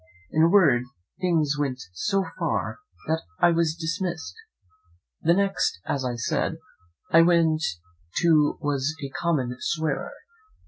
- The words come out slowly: Yes, slow, 130 wpm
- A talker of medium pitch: Yes, medium, 160 Hz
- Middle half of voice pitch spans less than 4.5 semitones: Yes, average, 2.9 semitones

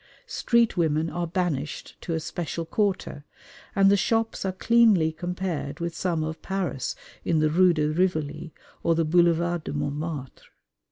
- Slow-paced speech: No, average, 155 wpm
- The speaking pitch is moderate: Yes, medium, 170 Hz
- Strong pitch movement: No, average, 3.0 semitones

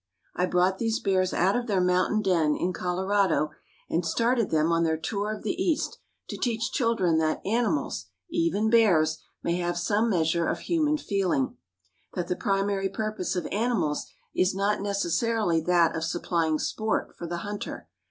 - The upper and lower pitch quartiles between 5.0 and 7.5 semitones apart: No, average, 4.0 semitones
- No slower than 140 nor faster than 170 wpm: Yes, average, 165 wpm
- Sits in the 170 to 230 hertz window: Yes, high, 190 Hz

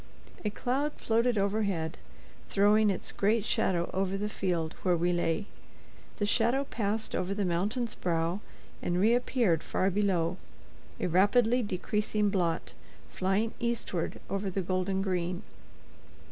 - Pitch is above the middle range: Yes, high, 195 Hz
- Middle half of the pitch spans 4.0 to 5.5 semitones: No, average, 3.4 semitones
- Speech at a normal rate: No, slow, 130 wpm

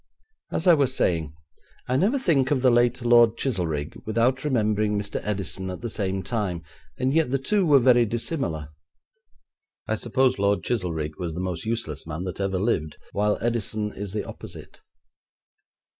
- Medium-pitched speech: No, low, 110 Hz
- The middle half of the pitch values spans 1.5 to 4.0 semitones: No, wide, 5.6 semitones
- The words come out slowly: No, average, 165 wpm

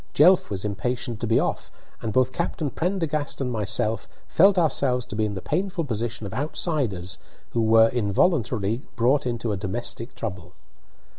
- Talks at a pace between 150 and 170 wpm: Yes, average, 160 wpm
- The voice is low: Yes, low, 120 Hz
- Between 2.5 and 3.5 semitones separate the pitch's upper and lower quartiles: No, average, 5.3 semitones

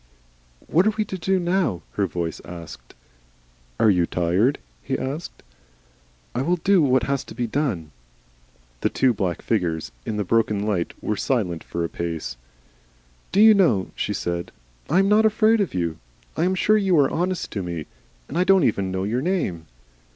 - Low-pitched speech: Yes, low, 120 Hz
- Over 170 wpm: Yes, average, 185 wpm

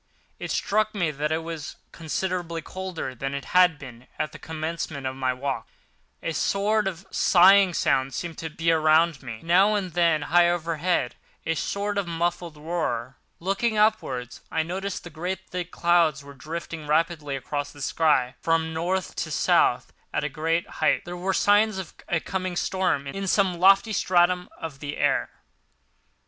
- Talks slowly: No, average, 165 wpm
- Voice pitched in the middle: Yes, medium, 165 Hz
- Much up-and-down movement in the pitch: No, average, 3.6 semitones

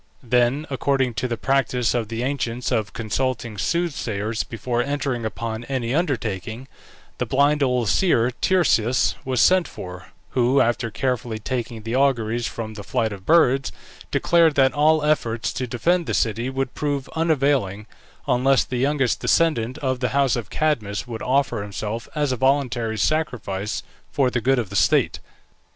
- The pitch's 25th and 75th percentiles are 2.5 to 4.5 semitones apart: Yes, average, 3.5 semitones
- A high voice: No, low, 125 Hz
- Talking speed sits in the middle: Yes, average, 160 wpm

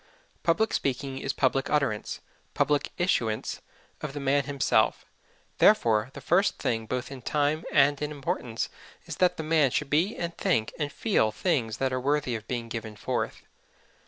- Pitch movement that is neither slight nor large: Yes, average, 4.2 semitones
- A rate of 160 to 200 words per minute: Yes, average, 165 wpm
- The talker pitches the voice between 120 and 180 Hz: Yes, medium, 140 Hz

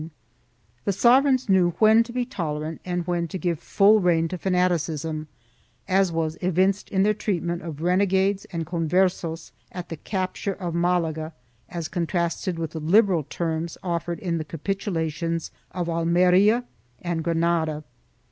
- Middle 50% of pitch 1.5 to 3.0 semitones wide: Yes, narrow, 2.6 semitones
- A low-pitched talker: No, medium, 175 Hz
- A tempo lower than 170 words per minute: Yes, average, 145 wpm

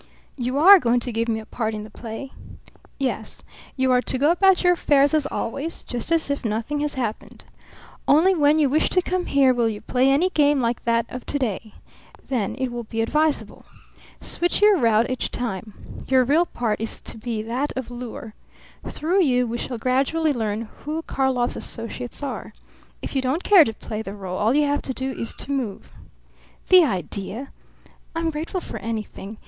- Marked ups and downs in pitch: No, average, 4.5 semitones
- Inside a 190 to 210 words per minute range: Yes, average, 195 wpm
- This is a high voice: Yes, very high, 255 Hz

